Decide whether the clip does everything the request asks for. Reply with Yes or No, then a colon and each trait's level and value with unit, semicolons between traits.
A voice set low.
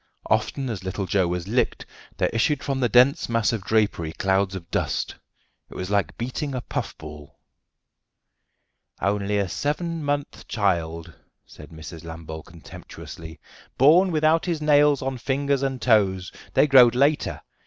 Yes: low, 110 Hz